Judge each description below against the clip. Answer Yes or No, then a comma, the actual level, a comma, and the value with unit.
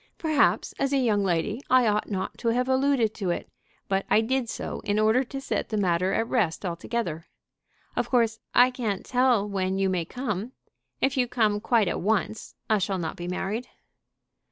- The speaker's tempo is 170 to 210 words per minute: Yes, average, 190 wpm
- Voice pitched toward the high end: Yes, high, 220 Hz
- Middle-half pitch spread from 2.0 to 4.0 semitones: No, average, 4.4 semitones